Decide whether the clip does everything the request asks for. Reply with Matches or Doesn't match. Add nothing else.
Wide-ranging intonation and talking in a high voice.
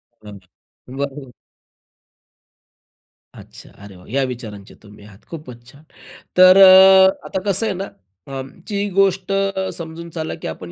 Doesn't match